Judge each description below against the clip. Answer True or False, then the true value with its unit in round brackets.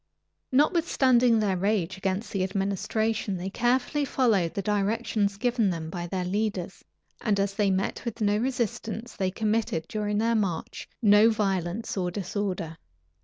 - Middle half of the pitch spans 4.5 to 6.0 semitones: False (3.1 semitones)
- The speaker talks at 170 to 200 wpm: False (145 wpm)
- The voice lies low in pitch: False (205 Hz)